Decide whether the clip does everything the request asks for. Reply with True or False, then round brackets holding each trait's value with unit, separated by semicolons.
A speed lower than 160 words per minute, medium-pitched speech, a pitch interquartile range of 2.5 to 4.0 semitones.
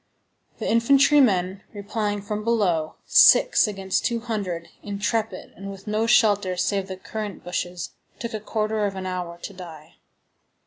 False (150 wpm; 200 Hz; 2.9 semitones)